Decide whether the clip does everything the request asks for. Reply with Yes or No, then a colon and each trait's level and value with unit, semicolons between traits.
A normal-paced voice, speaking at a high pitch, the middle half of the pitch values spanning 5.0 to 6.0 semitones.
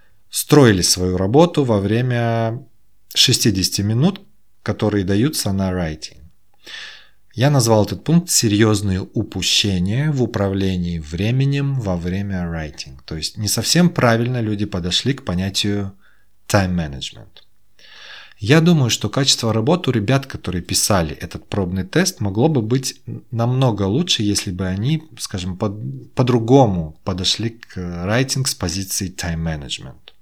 No: average, 125 wpm; low, 105 Hz; wide, 5.5 semitones